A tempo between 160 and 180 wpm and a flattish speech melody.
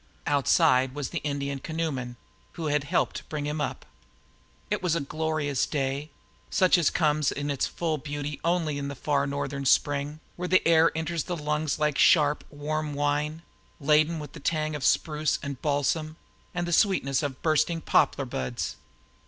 Yes: average, 175 wpm; narrow, 1.9 semitones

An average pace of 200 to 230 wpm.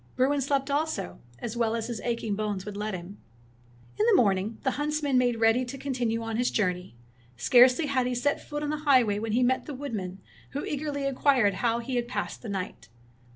Yes: fast, 205 wpm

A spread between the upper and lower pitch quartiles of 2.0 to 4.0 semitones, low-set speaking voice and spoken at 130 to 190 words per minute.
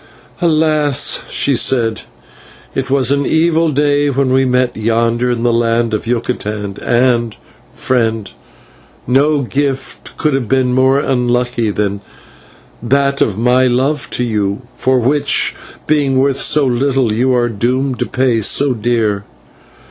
Yes: average, 2.9 semitones; low, 125 Hz; average, 140 wpm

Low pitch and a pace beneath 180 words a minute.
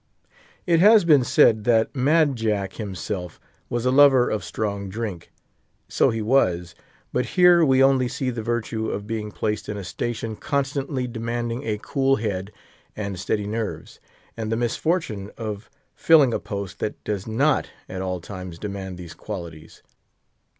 Yes: low, 110 Hz; average, 155 wpm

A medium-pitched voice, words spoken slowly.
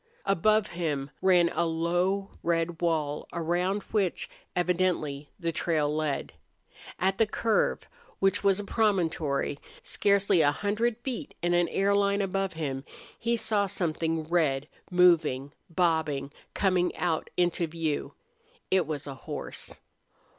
Yes: medium, 175 Hz; slow, 130 wpm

